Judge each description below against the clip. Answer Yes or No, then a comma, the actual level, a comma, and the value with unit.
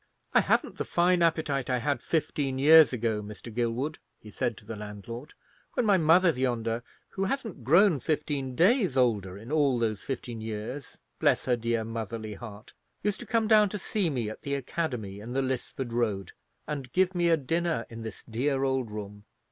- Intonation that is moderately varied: No, wide, 6.0 semitones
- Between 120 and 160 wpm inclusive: No, average, 180 wpm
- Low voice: Yes, low, 130 Hz